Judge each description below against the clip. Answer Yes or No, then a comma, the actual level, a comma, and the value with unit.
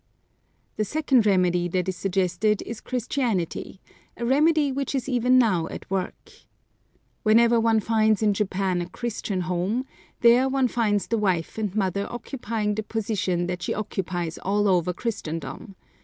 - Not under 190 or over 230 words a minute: No, average, 150 wpm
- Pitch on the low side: No, high, 210 Hz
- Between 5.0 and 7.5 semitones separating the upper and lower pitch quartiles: No, average, 4.3 semitones